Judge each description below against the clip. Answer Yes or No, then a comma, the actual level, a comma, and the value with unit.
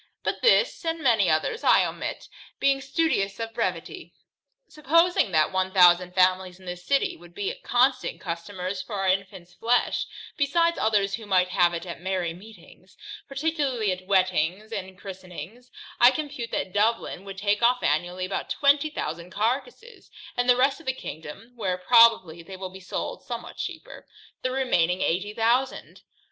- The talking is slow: No, average, 160 wpm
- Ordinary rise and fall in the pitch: No, wide, 5.7 semitones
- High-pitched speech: Yes, high, 200 Hz